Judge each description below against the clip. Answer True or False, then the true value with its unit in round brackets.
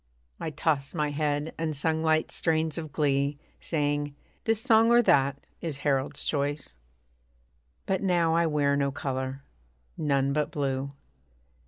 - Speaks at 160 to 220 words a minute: False (140 wpm)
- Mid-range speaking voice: True (145 Hz)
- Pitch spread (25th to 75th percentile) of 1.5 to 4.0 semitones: True (2.5 semitones)